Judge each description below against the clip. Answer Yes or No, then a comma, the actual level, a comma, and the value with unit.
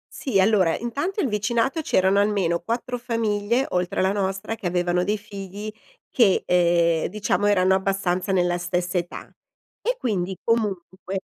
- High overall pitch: Yes, high, 195 Hz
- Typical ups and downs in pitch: Yes, average, 3.8 semitones